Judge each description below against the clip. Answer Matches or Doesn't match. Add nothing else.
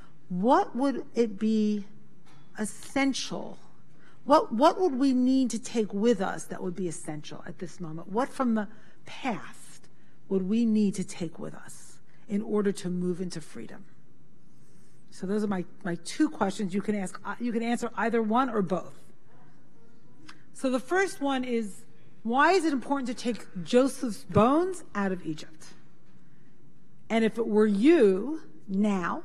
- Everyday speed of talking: Matches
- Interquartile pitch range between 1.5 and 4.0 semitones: Doesn't match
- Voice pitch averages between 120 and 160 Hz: Doesn't match